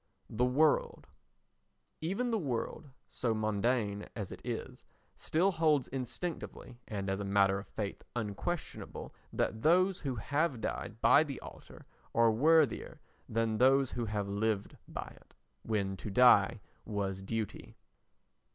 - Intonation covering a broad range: Yes, wide, 5.9 semitones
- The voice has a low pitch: Yes, low, 115 Hz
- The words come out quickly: No, slow, 135 wpm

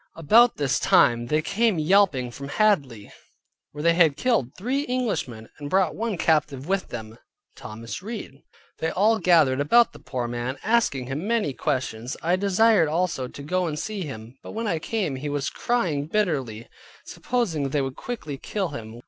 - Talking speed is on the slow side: No, average, 175 wpm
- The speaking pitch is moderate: Yes, medium, 155 Hz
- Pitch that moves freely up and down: Yes, wide, 7.5 semitones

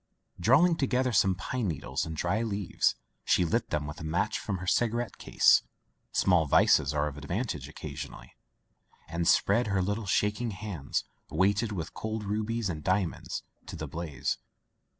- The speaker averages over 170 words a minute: No, average, 160 wpm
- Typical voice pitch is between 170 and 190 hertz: No, very low, 95 Hz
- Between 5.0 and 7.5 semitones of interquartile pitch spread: Yes, wide, 5.4 semitones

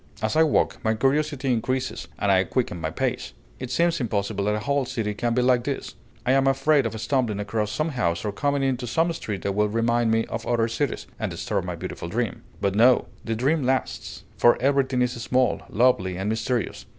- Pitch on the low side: Yes, low, 120 Hz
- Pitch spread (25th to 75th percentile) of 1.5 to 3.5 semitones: No, average, 3.9 semitones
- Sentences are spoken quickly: Yes, fast, 210 wpm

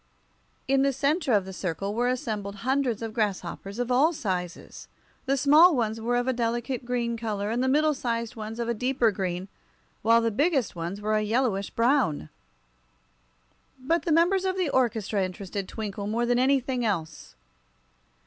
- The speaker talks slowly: No, average, 170 wpm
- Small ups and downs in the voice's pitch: No, average, 4.3 semitones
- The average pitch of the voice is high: Yes, high, 235 Hz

